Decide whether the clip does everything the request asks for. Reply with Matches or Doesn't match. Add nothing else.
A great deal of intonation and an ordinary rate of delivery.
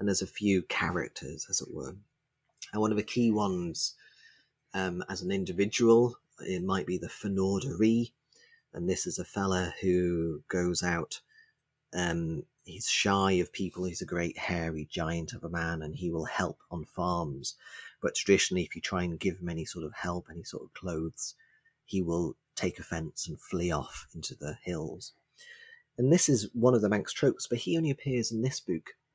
Matches